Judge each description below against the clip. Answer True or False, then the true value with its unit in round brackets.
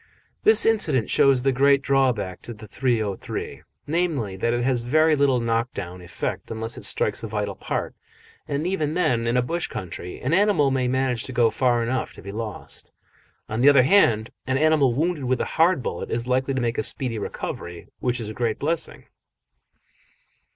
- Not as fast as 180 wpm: False (190 wpm)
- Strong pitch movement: False (3.7 semitones)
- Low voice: True (125 Hz)